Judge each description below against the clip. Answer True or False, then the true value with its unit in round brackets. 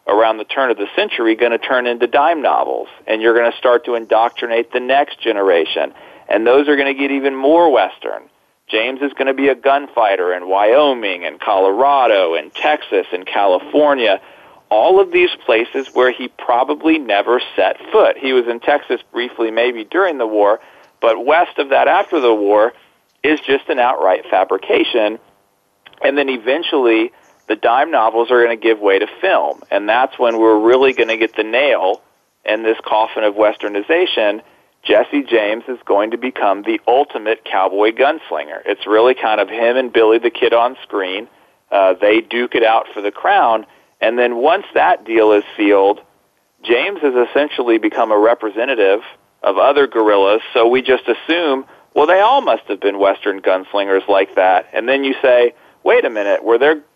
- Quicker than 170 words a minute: True (180 wpm)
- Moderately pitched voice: False (120 Hz)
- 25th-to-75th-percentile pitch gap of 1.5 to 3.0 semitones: False (4.0 semitones)